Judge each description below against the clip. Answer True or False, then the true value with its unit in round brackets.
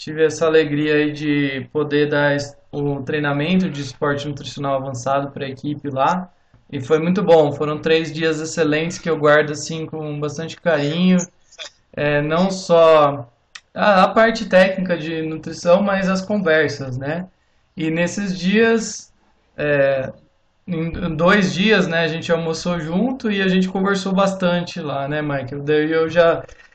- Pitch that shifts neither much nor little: True (3.3 semitones)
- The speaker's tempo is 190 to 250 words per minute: False (155 wpm)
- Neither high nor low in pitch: True (160 Hz)